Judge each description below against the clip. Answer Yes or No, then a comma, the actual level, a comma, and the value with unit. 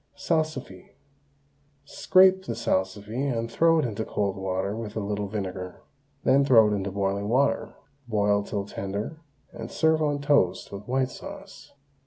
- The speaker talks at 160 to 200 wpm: No, average, 150 wpm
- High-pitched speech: No, low, 110 Hz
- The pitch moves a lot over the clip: Yes, wide, 5.9 semitones